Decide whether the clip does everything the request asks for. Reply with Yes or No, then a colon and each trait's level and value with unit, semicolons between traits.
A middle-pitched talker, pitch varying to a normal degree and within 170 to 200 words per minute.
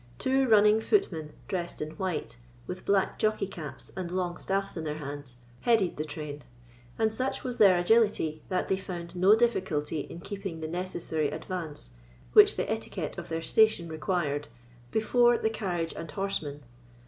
No: medium, 180 Hz; average, 4.9 semitones; average, 160 wpm